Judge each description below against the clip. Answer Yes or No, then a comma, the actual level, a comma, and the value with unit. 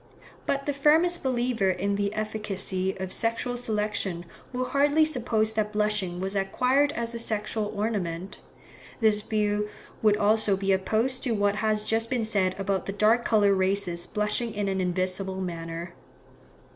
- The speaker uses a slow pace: No, average, 155 wpm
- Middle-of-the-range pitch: No, high, 210 Hz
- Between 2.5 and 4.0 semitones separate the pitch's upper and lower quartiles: Yes, average, 3.0 semitones